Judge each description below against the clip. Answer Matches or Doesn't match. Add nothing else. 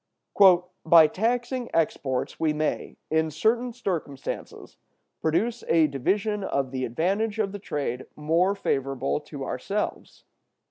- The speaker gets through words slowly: Matches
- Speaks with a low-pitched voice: Doesn't match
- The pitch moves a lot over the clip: Matches